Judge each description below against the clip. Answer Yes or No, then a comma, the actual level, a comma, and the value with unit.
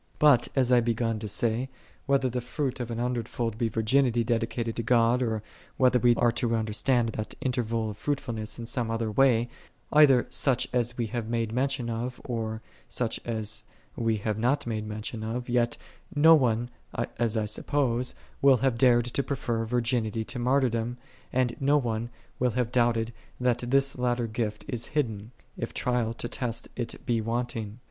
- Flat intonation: Yes, narrow, 1.8 semitones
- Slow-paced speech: No, average, 185 wpm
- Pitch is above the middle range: No, low, 120 Hz